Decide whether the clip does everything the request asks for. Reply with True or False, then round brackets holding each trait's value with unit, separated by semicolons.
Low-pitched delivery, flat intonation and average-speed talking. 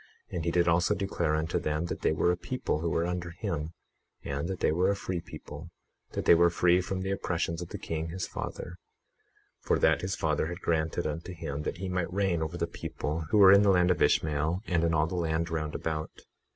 False (85 Hz; 2.1 semitones; 230 wpm)